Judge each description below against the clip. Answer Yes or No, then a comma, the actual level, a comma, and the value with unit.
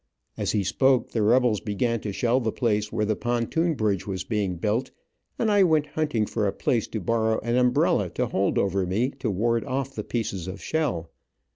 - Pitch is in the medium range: No, low, 115 Hz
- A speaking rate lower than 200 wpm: No, fast, 205 wpm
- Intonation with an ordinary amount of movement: Yes, average, 3.7 semitones